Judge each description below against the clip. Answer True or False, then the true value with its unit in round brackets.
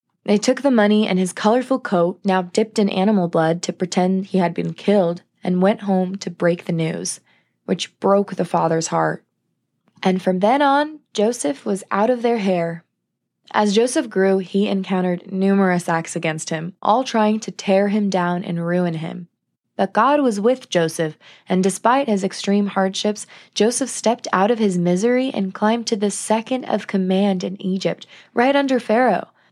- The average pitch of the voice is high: True (195 Hz)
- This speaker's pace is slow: False (175 wpm)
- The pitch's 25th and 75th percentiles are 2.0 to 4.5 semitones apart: True (3.3 semitones)